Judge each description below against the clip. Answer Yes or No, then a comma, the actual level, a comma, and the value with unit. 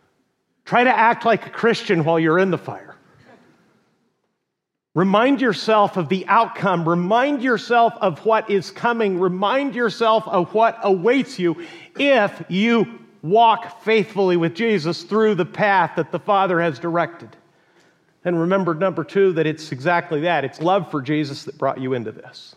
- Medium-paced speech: Yes, average, 155 wpm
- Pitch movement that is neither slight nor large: Yes, average, 4.8 semitones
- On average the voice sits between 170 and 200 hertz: Yes, high, 190 Hz